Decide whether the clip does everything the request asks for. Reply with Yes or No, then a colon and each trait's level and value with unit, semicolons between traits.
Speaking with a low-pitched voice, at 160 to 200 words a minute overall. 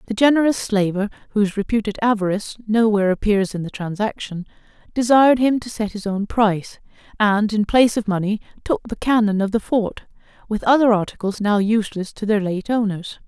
No: high, 215 Hz; average, 170 wpm